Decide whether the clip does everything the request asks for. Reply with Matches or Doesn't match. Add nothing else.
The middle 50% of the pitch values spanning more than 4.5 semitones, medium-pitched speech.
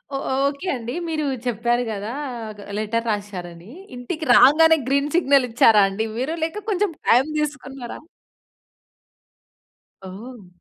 Doesn't match